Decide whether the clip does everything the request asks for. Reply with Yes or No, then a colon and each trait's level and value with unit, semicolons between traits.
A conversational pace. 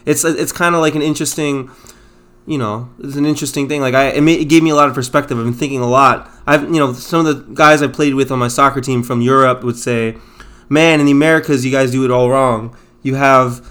No: fast, 260 wpm